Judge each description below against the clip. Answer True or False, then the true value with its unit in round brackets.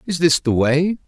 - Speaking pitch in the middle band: True (150 Hz)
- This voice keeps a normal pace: False (225 wpm)